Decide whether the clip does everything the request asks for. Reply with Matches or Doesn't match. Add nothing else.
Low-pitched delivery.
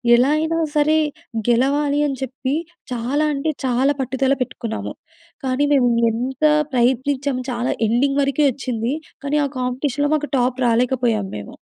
Doesn't match